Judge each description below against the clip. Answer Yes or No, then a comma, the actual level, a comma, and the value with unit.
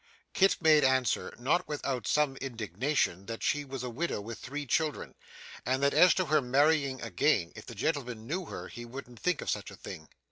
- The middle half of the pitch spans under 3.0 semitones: No, average, 4.1 semitones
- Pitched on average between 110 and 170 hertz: Yes, low, 135 Hz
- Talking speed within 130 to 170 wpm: No, average, 200 wpm